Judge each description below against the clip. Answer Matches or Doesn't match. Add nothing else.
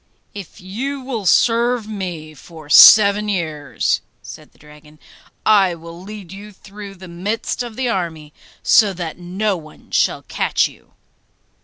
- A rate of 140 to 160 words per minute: Matches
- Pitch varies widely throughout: Doesn't match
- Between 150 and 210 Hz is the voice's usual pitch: Matches